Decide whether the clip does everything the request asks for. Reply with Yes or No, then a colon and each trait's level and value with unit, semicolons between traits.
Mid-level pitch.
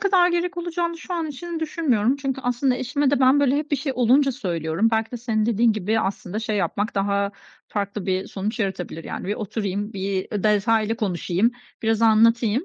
No: high, 225 Hz